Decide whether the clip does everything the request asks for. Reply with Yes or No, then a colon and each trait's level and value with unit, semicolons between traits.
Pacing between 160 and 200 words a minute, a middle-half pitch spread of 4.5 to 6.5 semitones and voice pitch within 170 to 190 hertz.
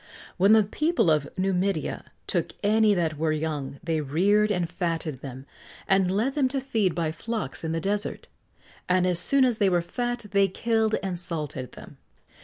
Yes: average, 180 wpm; average, 4.9 semitones; medium, 185 Hz